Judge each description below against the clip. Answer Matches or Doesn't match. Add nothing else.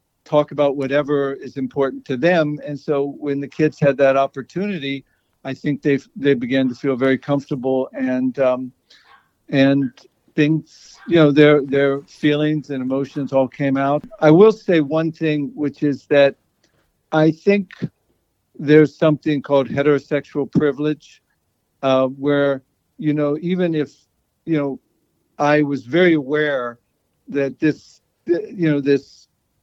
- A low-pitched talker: Doesn't match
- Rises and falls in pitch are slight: Matches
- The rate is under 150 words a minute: Matches